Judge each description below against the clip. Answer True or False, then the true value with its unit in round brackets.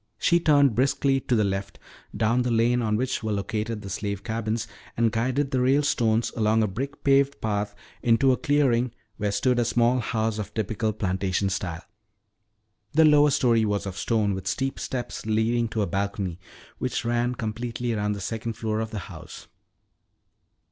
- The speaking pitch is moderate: False (115 Hz)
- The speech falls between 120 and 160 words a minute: False (175 wpm)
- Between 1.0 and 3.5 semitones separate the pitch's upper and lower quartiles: True (3.1 semitones)